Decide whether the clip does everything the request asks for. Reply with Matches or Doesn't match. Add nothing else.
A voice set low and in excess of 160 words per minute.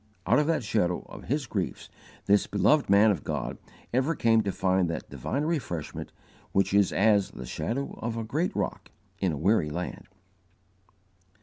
Matches